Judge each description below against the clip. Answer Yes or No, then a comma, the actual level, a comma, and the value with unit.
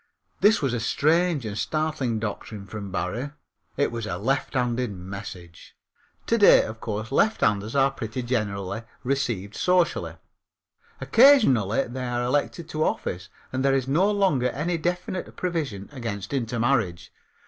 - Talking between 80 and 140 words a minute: Yes, slow, 135 wpm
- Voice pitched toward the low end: Yes, low, 125 Hz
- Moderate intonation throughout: No, wide, 6.2 semitones